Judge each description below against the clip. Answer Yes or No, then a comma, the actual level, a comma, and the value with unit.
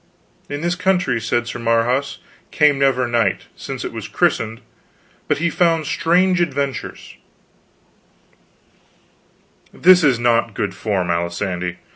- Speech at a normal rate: No, slow, 125 wpm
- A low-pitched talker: Yes, low, 130 Hz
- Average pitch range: No, wide, 6.4 semitones